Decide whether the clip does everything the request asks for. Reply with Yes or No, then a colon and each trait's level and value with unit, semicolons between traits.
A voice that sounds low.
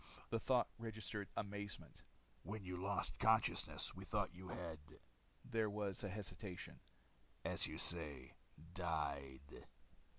Yes: very low, 95 Hz